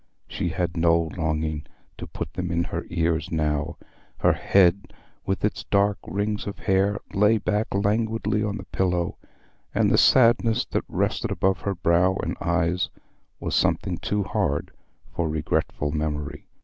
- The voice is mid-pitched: No, very low, 90 Hz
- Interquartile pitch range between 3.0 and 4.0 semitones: Yes, average, 3.7 semitones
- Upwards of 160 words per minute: No, average, 150 wpm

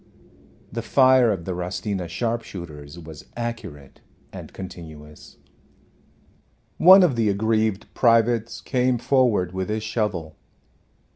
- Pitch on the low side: Yes, low, 105 Hz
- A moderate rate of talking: No, slow, 110 wpm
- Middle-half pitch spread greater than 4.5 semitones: Yes, average, 5.3 semitones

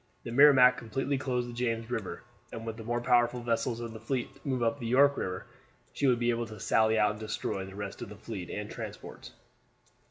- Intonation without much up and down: Yes, narrow, 2.2 semitones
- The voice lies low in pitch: Yes, low, 120 Hz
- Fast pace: Yes, fast, 230 wpm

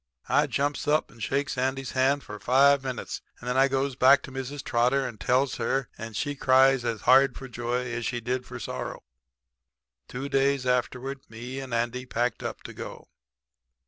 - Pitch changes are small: Yes, narrow, 1.8 semitones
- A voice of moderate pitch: No, low, 130 Hz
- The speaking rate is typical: Yes, average, 185 wpm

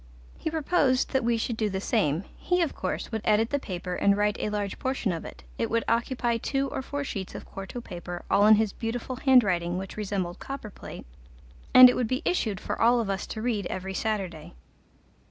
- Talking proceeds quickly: Yes, fast, 210 wpm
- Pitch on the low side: No, high, 220 Hz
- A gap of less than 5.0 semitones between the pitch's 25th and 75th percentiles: Yes, average, 4.6 semitones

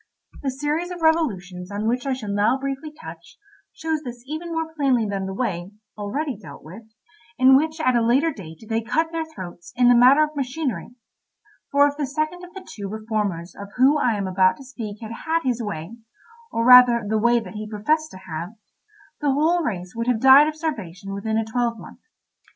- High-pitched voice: Yes, high, 245 Hz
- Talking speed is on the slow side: No, average, 200 wpm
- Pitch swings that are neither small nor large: No, wide, 6.4 semitones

